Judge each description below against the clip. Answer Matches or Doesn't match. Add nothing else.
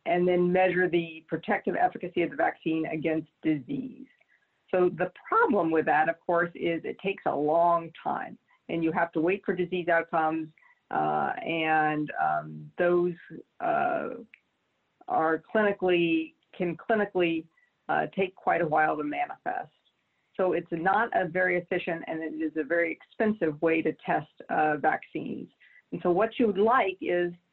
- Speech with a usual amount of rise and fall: Matches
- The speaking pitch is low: Doesn't match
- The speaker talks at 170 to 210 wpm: Doesn't match